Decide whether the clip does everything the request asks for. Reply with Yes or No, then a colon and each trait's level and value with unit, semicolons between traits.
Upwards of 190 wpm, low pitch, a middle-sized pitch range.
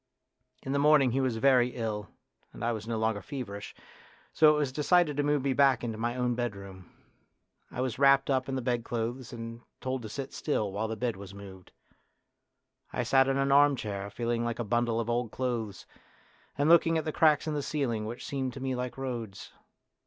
Yes: fast, 205 wpm; low, 125 Hz; average, 3.4 semitones